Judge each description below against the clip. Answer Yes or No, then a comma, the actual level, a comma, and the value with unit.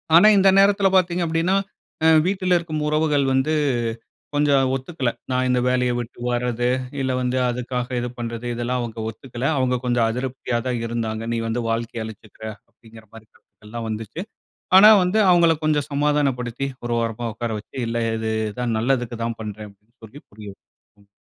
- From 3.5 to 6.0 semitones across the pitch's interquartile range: Yes, average, 4.1 semitones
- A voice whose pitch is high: No, low, 125 Hz